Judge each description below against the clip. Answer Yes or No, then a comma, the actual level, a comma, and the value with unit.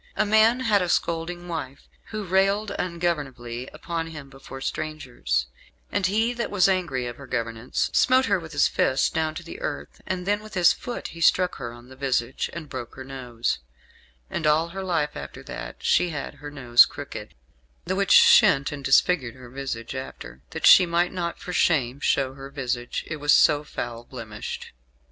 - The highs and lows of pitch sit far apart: Yes, wide, 5.7 semitones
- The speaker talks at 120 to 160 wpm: No, average, 185 wpm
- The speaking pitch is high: No, medium, 150 Hz